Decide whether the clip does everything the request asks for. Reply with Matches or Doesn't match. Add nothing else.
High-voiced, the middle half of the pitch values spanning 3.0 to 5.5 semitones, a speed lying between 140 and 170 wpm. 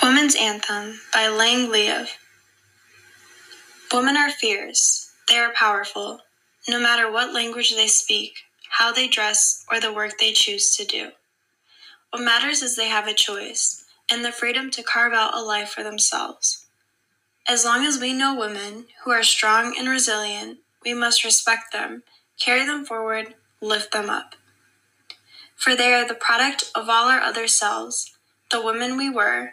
Doesn't match